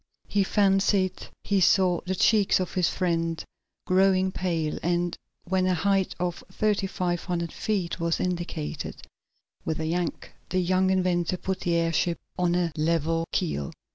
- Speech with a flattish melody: Yes, narrow, 2.0 semitones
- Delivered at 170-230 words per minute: No, average, 150 wpm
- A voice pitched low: No, medium, 180 Hz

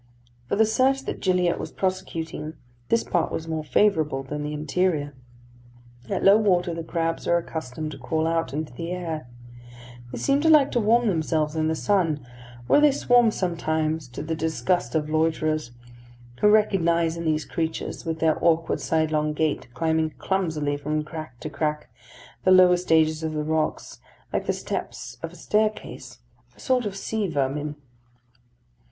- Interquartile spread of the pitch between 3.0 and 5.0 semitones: Yes, average, 3.3 semitones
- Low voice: No, medium, 160 Hz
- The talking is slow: No, average, 165 wpm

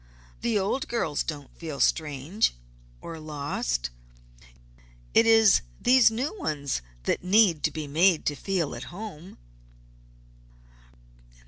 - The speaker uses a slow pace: Yes, slow, 115 wpm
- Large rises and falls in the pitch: Yes, wide, 6.8 semitones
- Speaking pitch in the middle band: Yes, medium, 165 Hz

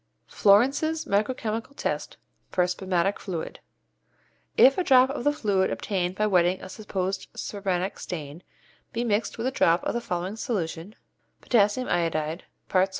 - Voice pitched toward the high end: Yes, high, 200 Hz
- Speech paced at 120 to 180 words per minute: Yes, average, 150 wpm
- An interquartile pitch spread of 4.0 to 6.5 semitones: Yes, average, 4.7 semitones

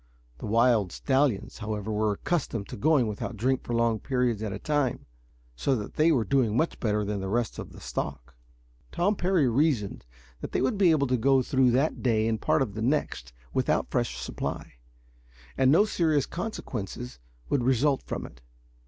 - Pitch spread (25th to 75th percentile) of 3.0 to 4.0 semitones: No, average, 5.1 semitones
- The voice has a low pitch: Yes, low, 125 Hz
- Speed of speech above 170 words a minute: Yes, average, 190 wpm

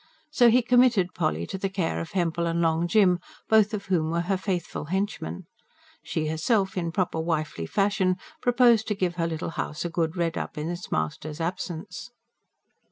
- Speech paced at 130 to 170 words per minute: No, average, 180 wpm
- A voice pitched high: No, medium, 175 Hz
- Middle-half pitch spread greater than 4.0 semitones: No, average, 3.5 semitones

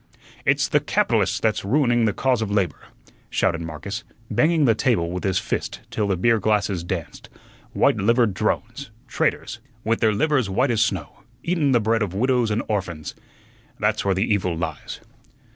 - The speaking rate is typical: Yes, average, 170 wpm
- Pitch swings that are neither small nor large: Yes, average, 3.9 semitones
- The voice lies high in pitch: No, low, 105 Hz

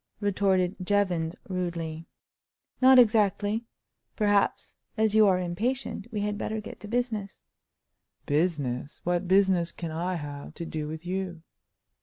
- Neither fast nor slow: No, slow, 130 wpm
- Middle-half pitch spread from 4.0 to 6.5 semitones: No, average, 3.6 semitones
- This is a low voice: No, medium, 185 Hz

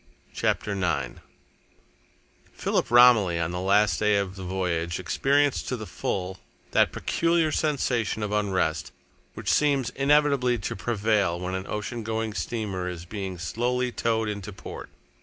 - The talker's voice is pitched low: Yes, low, 105 Hz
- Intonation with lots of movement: No, average, 4.7 semitones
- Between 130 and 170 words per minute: Yes, average, 140 wpm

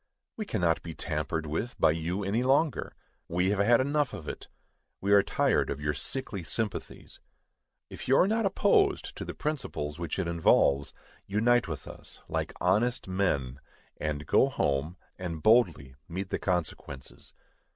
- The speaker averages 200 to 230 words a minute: No, average, 160 wpm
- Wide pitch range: Yes, wide, 7.6 semitones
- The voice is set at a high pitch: No, very low, 95 Hz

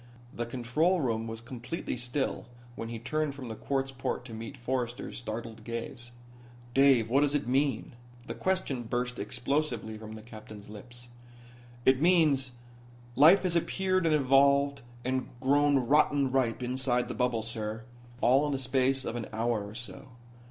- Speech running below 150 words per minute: No, average, 160 wpm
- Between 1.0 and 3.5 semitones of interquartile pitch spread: Yes, average, 3.2 semitones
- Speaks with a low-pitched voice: Yes, low, 125 Hz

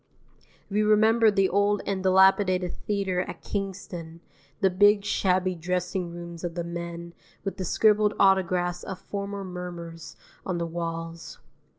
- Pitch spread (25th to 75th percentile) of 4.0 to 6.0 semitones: No, narrow, 2.6 semitones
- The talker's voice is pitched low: No, medium, 185 Hz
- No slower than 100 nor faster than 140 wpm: Yes, slow, 135 wpm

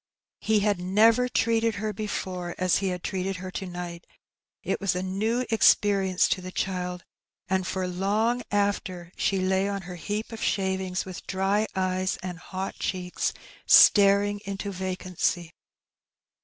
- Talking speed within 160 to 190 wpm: No, average, 150 wpm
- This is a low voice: No, high, 190 Hz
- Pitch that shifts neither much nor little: No, narrow, 1.9 semitones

